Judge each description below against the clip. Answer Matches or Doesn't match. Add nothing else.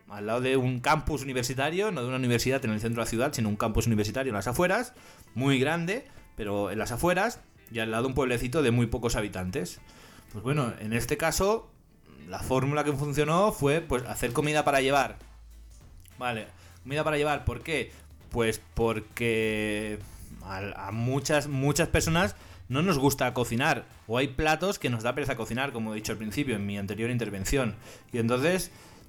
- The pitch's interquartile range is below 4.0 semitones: Doesn't match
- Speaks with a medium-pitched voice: Doesn't match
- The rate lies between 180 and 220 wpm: Matches